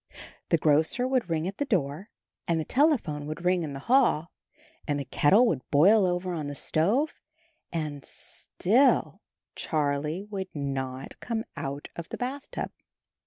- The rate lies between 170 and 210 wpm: No, average, 155 wpm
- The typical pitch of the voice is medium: Yes, medium, 170 Hz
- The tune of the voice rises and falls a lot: Yes, wide, 6.8 semitones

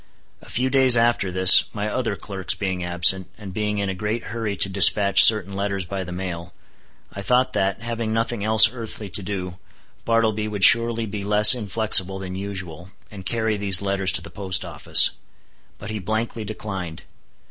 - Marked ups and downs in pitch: No, average, 2.7 semitones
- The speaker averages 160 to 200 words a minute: Yes, average, 180 wpm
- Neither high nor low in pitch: No, low, 100 Hz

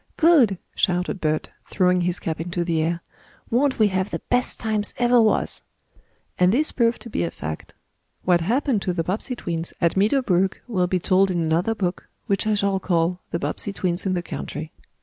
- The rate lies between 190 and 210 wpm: Yes, average, 195 wpm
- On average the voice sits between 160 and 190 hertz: Yes, medium, 185 Hz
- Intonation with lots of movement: No, average, 4.0 semitones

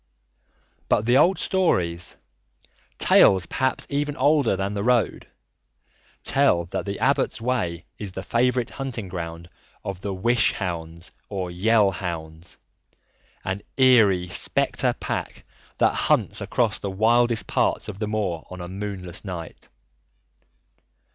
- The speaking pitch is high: No, low, 100 Hz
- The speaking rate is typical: No, slow, 125 wpm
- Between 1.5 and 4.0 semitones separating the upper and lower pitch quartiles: No, average, 5.2 semitones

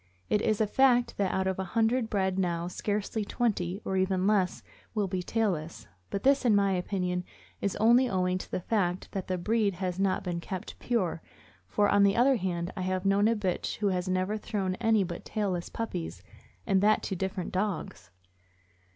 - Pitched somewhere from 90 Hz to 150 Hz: No, high, 190 Hz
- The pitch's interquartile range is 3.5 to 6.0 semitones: No, average, 2.7 semitones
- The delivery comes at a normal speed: Yes, average, 195 wpm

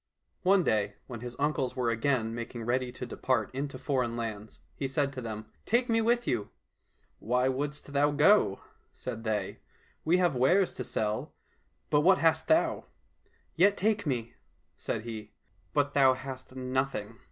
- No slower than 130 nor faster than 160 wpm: No, average, 185 wpm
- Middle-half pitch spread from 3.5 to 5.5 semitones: Yes, average, 4.2 semitones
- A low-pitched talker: Yes, low, 130 Hz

